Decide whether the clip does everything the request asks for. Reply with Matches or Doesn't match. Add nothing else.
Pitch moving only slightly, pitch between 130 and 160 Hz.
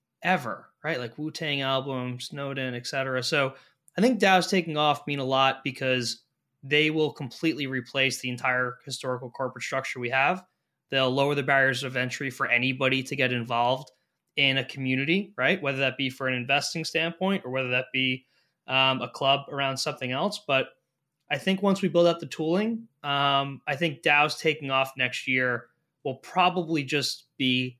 Doesn't match